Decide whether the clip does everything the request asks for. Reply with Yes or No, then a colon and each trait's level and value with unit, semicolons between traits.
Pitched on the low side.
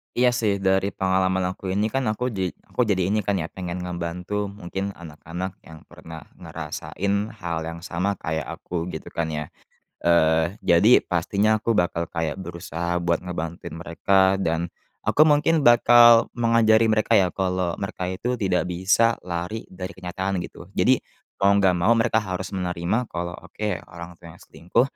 Yes: very low, 95 Hz